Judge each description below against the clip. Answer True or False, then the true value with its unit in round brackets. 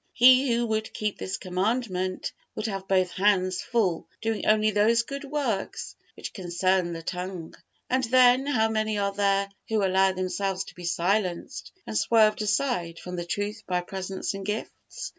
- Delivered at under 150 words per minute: False (165 wpm)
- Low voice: False (200 Hz)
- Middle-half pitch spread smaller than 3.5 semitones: True (3.1 semitones)